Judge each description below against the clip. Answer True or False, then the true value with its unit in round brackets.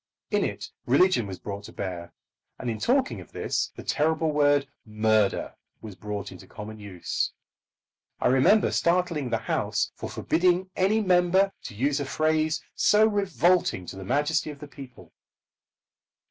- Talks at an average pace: True (155 wpm)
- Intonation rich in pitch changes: True (8.7 semitones)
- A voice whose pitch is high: False (145 Hz)